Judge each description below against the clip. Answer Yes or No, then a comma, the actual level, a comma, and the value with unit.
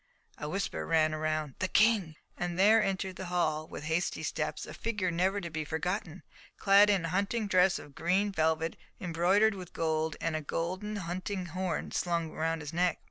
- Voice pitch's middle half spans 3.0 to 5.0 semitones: Yes, average, 3.3 semitones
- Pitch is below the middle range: No, medium, 175 Hz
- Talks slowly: No, average, 185 wpm